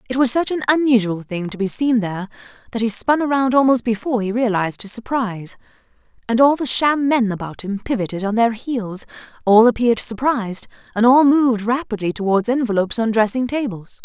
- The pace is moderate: Yes, average, 185 wpm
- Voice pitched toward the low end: No, high, 230 Hz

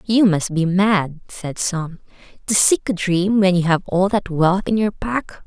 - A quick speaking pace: Yes, fast, 210 wpm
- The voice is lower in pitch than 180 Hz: No, high, 190 Hz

